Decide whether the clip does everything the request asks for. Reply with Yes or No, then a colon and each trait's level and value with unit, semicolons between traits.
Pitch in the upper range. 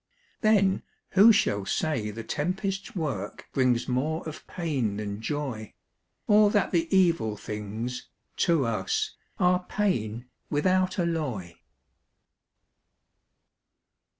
No: medium, 150 Hz